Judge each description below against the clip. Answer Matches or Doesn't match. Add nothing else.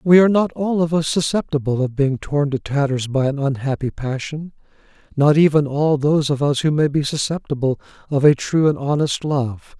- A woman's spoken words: Doesn't match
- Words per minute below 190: Doesn't match